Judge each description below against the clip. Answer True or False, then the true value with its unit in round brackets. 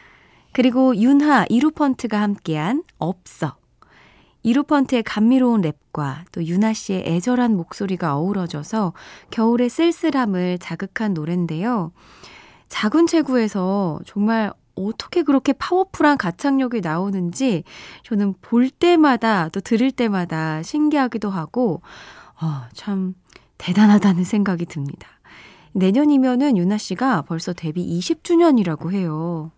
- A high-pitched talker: True (210 Hz)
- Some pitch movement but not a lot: False (6.6 semitones)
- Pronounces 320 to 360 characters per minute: False (275 characters per minute)